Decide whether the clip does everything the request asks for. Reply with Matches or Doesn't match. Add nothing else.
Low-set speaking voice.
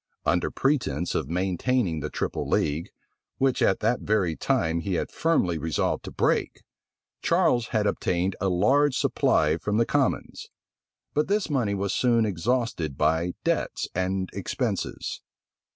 Matches